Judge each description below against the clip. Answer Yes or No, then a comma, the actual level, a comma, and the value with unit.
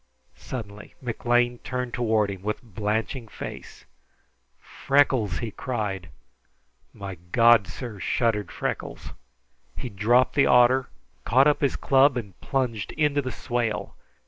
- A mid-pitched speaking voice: No, low, 120 Hz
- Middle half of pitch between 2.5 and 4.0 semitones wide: Yes, average, 3.4 semitones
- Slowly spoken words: Yes, slow, 120 wpm